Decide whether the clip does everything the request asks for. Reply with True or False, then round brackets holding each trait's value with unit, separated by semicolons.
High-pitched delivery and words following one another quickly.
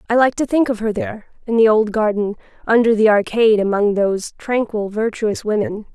False (220 Hz; 190 wpm)